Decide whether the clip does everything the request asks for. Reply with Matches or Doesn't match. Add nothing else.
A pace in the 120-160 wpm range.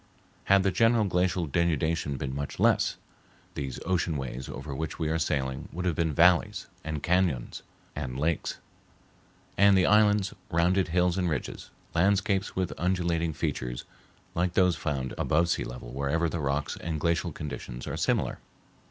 Matches